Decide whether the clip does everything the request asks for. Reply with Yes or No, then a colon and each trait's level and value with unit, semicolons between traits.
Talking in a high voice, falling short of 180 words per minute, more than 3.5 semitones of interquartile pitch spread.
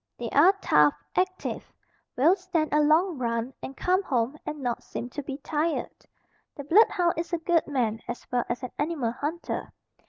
No: very high, 295 Hz; average, 185 wpm; wide, 5.6 semitones